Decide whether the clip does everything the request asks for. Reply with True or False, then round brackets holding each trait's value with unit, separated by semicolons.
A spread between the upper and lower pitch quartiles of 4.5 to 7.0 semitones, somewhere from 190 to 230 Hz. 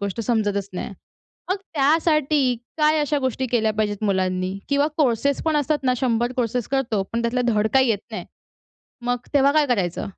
False (4.8 semitones; 245 Hz)